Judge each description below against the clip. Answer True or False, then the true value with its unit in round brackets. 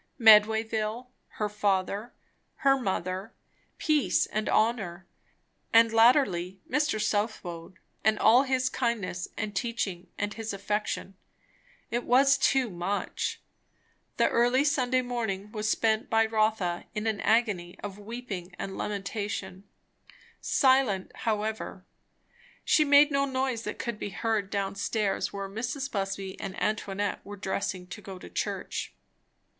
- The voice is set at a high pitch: True (215 Hz)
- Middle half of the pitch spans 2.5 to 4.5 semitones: True (3.4 semitones)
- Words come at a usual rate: False (130 wpm)